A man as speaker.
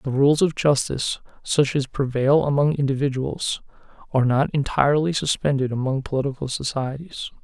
Yes: male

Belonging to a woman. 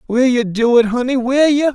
No: male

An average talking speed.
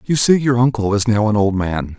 No: fast, 270 wpm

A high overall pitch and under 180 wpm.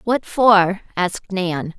Yes: high, 195 Hz; slow, 135 wpm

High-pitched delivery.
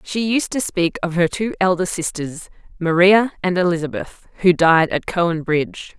No: medium, 180 Hz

